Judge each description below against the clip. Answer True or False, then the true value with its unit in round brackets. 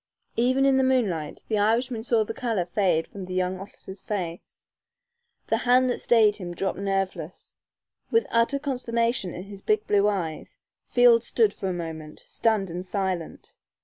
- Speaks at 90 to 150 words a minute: False (165 wpm)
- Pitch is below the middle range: False (205 Hz)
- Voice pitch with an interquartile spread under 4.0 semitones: False (4.5 semitones)